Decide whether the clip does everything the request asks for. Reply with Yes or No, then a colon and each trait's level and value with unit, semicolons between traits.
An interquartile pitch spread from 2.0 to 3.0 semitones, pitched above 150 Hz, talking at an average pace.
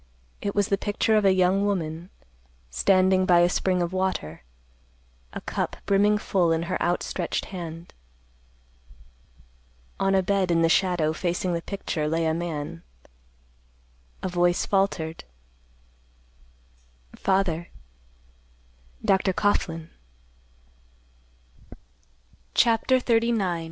No: average, 2.7 semitones; medium, 185 Hz; slow, 105 wpm